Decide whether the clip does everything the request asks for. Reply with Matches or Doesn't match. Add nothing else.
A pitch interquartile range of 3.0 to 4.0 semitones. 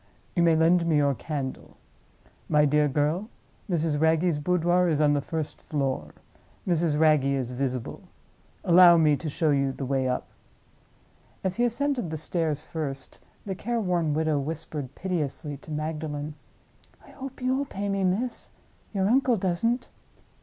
Matches